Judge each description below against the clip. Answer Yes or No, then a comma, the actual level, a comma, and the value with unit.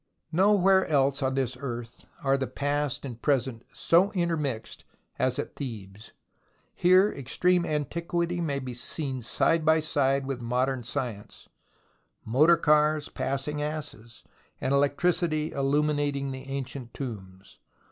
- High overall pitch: No, medium, 140 Hz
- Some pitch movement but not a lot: Yes, average, 3.3 semitones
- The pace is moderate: No, slow, 125 wpm